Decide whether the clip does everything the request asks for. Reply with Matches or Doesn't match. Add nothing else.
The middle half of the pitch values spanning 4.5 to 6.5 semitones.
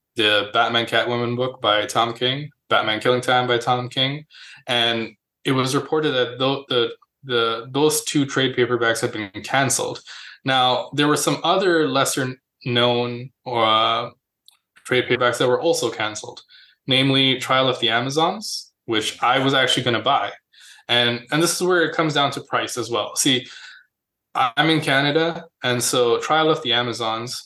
Doesn't match